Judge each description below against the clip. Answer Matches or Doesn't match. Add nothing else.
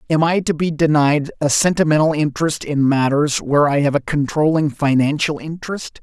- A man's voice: Matches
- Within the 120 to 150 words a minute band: Doesn't match